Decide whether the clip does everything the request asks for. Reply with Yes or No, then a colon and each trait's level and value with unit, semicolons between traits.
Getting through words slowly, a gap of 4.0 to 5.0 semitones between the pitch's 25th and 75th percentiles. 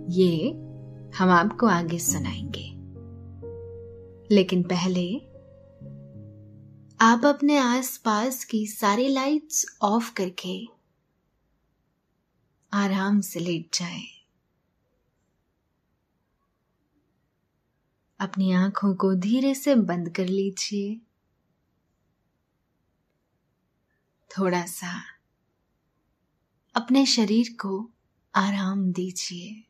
Yes: slow, 70 wpm; average, 4.6 semitones